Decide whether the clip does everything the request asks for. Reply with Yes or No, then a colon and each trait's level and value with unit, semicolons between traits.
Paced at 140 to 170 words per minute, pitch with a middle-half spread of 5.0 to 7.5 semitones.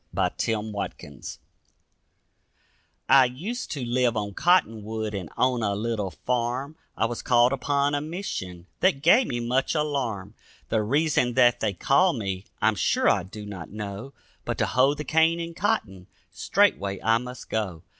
Yes: average, 160 wpm; wide, 5.5 semitones